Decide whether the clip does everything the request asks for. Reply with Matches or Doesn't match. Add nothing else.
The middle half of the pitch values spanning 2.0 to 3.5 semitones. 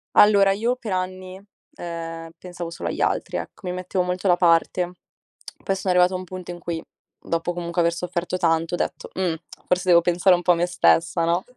Doesn't match